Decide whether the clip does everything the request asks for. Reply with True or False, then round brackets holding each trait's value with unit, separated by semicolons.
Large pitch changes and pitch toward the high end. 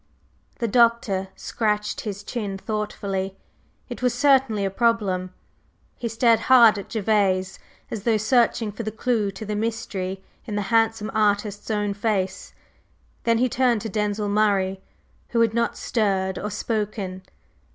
False (2.5 semitones; 210 Hz)